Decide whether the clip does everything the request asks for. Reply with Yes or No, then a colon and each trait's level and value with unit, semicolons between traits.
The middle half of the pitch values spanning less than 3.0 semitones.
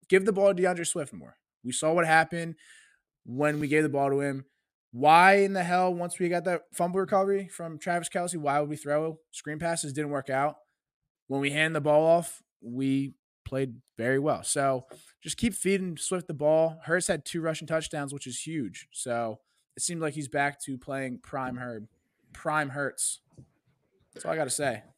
No: average, 3.8 semitones